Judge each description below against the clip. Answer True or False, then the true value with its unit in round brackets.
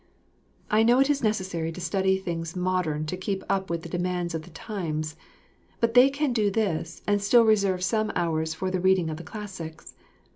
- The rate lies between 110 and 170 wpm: False (195 wpm)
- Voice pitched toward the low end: False (185 Hz)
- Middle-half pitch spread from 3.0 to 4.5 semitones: True (4.2 semitones)